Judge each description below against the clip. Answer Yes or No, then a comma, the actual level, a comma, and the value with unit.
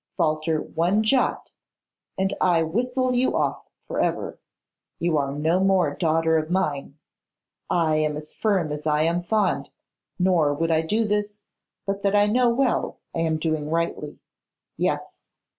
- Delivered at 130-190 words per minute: Yes, average, 155 wpm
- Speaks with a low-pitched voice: No, medium, 170 Hz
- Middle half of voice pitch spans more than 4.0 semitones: Yes, average, 4.7 semitones